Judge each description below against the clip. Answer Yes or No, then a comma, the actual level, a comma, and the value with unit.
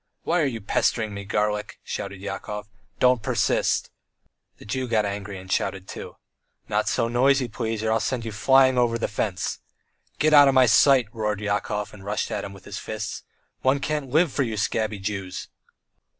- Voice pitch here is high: No, low, 110 Hz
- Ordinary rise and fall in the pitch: Yes, average, 4.0 semitones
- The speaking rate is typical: Yes, average, 185 wpm